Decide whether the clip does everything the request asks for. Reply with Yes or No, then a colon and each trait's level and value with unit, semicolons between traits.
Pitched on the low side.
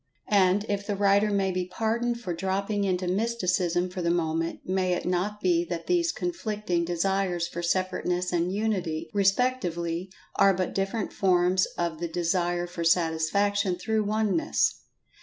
No: medium, 185 Hz